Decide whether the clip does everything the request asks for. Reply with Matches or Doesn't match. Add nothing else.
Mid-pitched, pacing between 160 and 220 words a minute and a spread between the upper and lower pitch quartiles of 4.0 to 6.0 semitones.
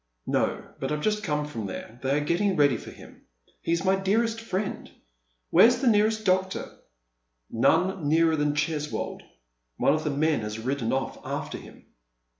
Matches